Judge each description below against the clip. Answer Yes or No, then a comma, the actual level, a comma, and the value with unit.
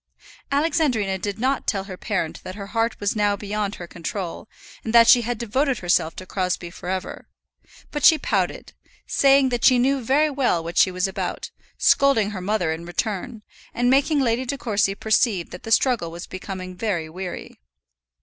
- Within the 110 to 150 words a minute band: No, average, 180 wpm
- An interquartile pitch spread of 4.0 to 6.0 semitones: Yes, average, 5.2 semitones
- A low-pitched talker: No, high, 210 Hz